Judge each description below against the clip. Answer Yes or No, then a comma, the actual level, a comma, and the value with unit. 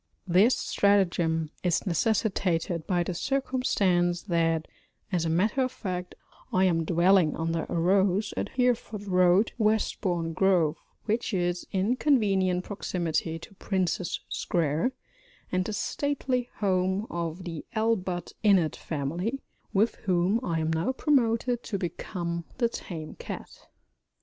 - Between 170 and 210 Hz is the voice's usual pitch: Yes, medium, 185 Hz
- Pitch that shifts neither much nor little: Yes, average, 4.0 semitones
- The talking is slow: Yes, slow, 130 wpm